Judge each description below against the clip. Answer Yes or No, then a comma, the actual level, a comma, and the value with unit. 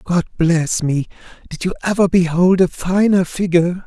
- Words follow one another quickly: No, average, 155 wpm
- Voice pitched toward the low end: No, medium, 180 Hz